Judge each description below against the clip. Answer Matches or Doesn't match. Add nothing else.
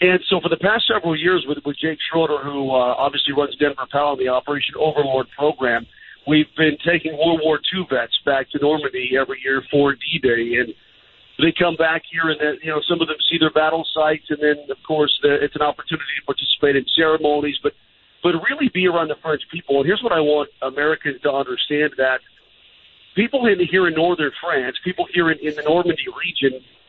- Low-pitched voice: Doesn't match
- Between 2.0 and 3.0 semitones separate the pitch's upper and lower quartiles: Matches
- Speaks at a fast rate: Matches